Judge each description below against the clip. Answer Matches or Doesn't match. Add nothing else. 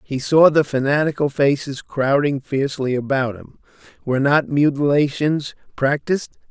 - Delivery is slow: Matches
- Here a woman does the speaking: Doesn't match